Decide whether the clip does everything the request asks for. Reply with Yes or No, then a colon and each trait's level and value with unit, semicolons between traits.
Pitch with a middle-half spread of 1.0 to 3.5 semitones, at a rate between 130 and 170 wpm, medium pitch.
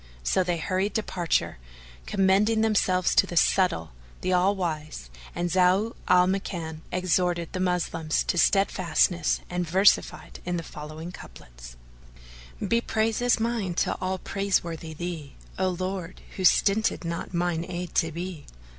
Yes: average, 2.7 semitones; average, 145 wpm; medium, 180 Hz